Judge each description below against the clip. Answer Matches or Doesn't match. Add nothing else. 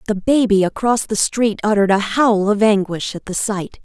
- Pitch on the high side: Matches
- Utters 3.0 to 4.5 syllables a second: Doesn't match